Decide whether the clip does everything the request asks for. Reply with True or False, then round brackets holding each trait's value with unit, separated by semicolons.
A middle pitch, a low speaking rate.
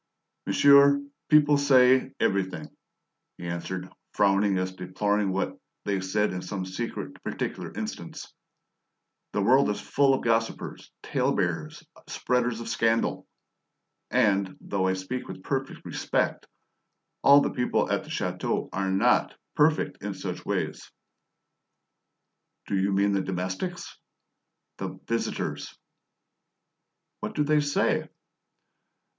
False (105 Hz; 125 wpm)